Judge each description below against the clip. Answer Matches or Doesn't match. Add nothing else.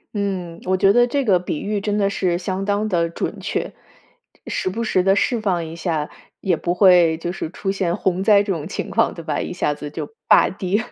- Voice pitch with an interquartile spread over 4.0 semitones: Doesn't match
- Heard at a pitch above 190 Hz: Doesn't match